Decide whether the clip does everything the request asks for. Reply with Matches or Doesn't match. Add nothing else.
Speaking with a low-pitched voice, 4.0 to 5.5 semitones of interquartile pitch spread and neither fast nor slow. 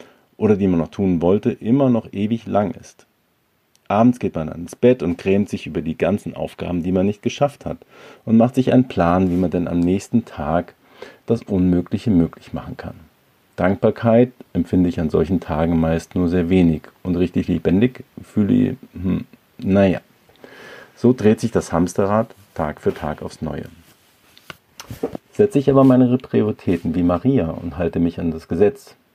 Matches